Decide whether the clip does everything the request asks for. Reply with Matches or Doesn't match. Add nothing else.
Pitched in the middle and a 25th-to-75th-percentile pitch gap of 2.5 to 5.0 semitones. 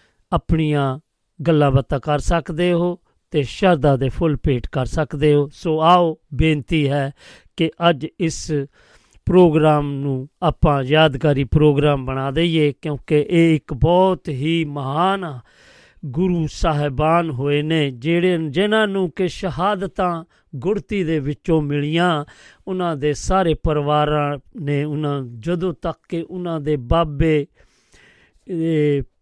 Matches